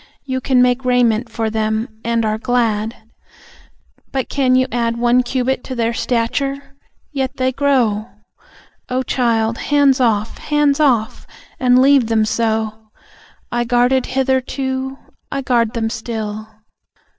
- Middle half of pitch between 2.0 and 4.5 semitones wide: Yes, narrow, 2.6 semitones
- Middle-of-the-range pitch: No, high, 245 Hz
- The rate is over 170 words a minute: No, slow, 135 wpm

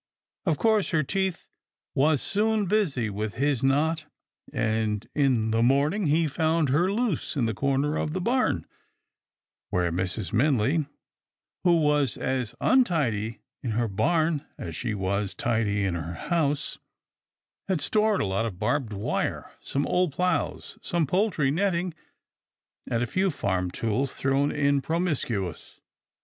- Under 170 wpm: Yes, average, 145 wpm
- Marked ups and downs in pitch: Yes, wide, 7.2 semitones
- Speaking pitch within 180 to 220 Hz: No, medium, 140 Hz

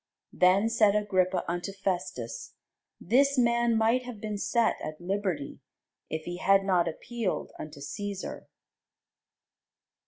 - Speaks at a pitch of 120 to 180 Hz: No, high, 195 Hz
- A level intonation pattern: No, average, 4.2 semitones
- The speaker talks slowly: Yes, slow, 120 wpm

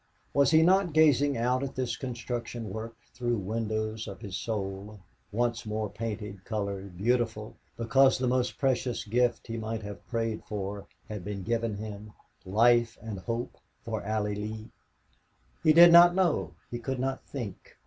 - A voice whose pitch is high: No, low, 115 Hz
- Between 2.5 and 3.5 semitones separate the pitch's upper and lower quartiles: Yes, average, 3.0 semitones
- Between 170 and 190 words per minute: No, average, 160 wpm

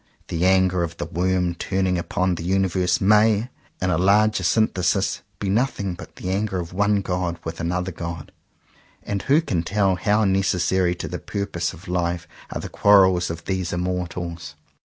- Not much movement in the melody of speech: Yes, narrow, 2.2 semitones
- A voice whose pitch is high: No, very low, 90 Hz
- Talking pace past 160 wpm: Yes, average, 170 wpm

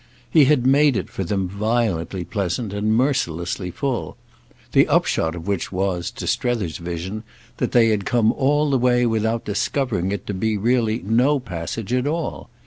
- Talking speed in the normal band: Yes, average, 170 wpm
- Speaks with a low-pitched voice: Yes, low, 110 Hz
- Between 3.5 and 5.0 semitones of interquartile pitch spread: Yes, average, 4.7 semitones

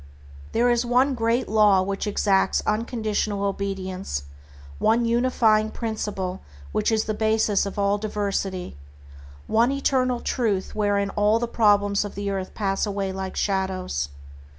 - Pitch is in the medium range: No, high, 205 Hz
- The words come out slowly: Yes, slow, 130 wpm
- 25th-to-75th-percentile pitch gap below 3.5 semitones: Yes, narrow, 2.5 semitones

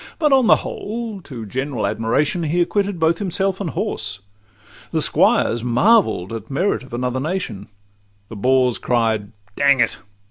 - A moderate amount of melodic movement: No, wide, 8.7 semitones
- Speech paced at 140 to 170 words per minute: Yes, average, 150 wpm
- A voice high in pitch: No, low, 135 Hz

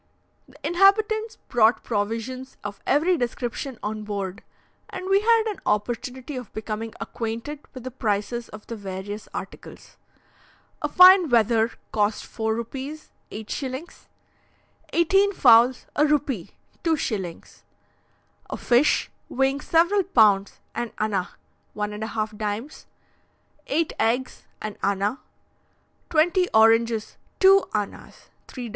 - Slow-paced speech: Yes, slow, 110 wpm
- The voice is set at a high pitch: Yes, high, 240 Hz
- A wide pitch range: Yes, wide, 5.9 semitones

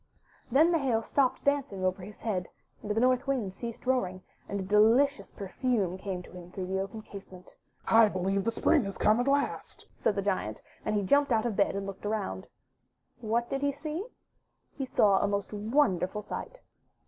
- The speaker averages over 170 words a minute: Yes, average, 195 wpm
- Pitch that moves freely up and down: No, average, 4.9 semitones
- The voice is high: Yes, high, 215 Hz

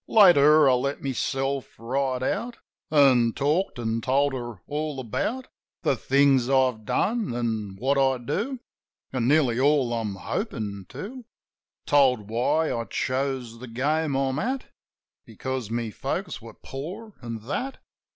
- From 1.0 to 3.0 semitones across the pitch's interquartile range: No, average, 4.0 semitones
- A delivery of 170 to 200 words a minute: No, average, 140 wpm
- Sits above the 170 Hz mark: No, low, 135 Hz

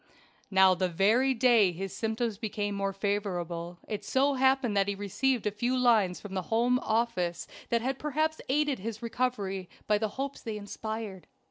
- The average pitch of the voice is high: Yes, high, 215 Hz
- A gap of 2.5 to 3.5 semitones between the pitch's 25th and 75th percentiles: No, average, 4.2 semitones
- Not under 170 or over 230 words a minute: Yes, average, 175 wpm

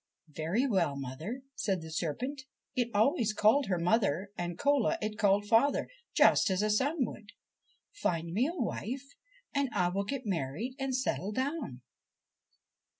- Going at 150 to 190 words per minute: Yes, average, 155 wpm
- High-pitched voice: Yes, high, 215 Hz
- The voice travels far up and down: Yes, wide, 6.8 semitones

